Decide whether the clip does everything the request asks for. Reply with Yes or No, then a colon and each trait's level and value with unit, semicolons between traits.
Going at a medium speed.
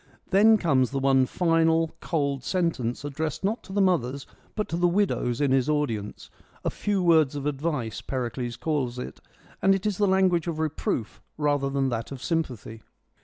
Yes: average, 180 wpm